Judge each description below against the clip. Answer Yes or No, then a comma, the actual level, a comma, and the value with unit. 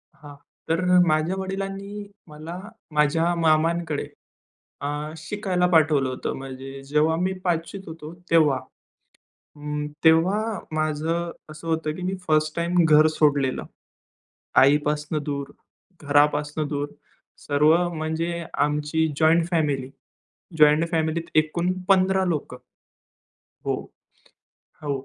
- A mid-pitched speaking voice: Yes, medium, 155 Hz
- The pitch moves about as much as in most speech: No, narrow, 2.3 semitones